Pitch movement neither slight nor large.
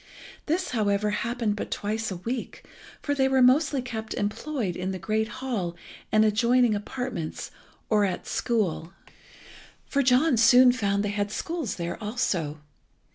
Yes: average, 3.8 semitones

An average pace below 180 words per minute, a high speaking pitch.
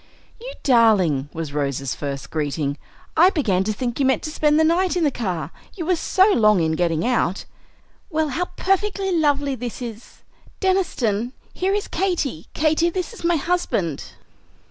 Yes: average, 165 wpm; very high, 265 Hz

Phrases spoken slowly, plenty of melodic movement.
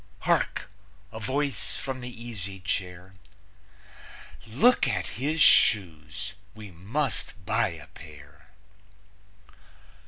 Yes: slow, 95 wpm; wide, 6.3 semitones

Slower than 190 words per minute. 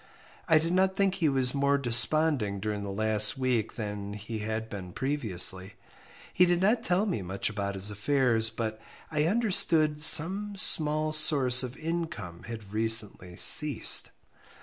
Yes: average, 150 wpm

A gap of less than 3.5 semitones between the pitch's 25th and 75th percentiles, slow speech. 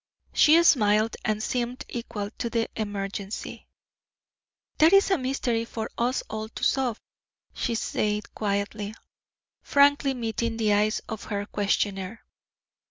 Yes: average, 2.9 semitones; slow, 125 wpm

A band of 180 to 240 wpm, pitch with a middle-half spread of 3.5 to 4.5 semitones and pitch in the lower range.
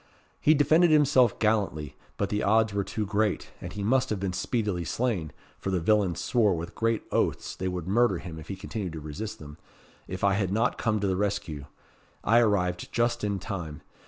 Yes: average, 200 wpm; average, 3.8 semitones; low, 100 Hz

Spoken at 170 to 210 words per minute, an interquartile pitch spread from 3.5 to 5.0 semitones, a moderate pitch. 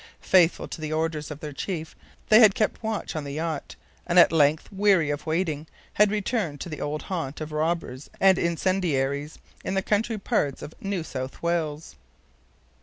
Yes: average, 180 wpm; average, 4.1 semitones; medium, 160 Hz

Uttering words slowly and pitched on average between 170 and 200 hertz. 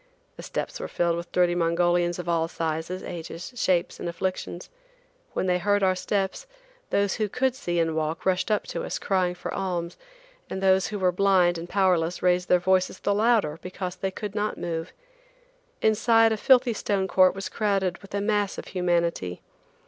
No: average, 185 wpm; medium, 185 Hz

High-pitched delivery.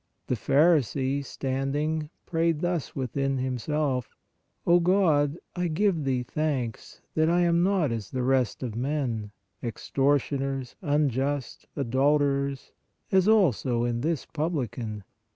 No: medium, 140 Hz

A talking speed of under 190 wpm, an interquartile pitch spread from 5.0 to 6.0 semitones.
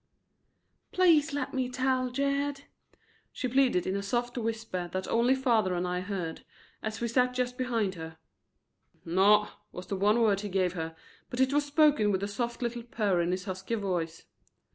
Yes: average, 175 wpm; average, 5.3 semitones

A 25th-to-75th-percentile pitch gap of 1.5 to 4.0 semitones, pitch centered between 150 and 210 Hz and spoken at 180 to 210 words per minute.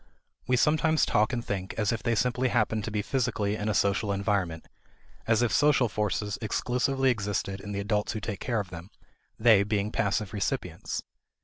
No: average, 3.0 semitones; low, 105 Hz; average, 185 wpm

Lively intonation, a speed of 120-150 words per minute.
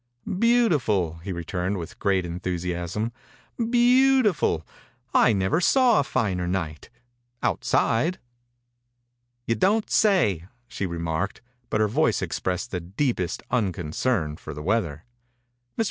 Yes: wide, 8.8 semitones; slow, 135 wpm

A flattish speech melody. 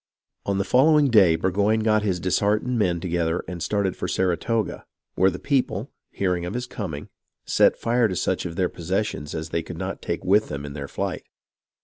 No: average, 4.0 semitones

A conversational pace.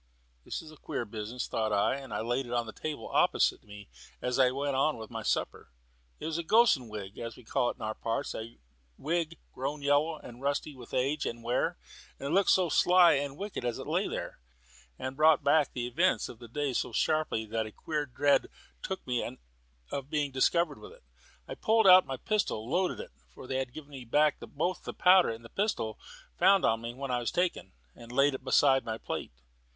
No: fast, 215 wpm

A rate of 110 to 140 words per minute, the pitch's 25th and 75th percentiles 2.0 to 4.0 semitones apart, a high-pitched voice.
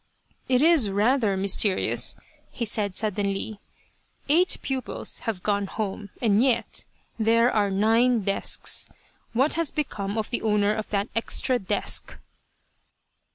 Yes: slow, 135 wpm; average, 3.4 semitones; high, 215 Hz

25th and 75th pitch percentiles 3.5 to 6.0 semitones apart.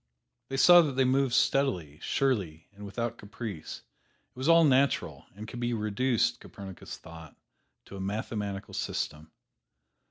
Yes: average, 5.2 semitones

